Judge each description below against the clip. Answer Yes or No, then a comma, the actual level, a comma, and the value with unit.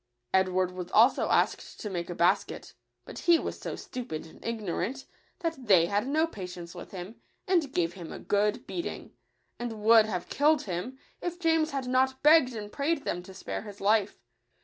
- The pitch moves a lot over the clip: Yes, wide, 7.0 semitones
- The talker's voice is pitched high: Yes, high, 220 Hz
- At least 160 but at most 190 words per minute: Yes, average, 185 wpm